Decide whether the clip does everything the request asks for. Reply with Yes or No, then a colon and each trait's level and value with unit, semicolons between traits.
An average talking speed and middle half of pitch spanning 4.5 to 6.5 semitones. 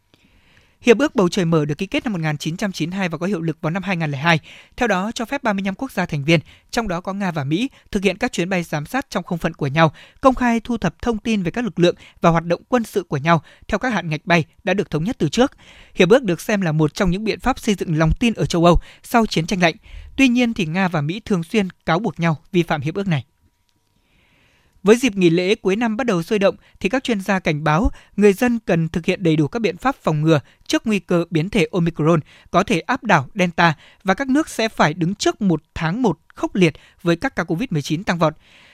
No: fast, 255 wpm; average, 5.1 semitones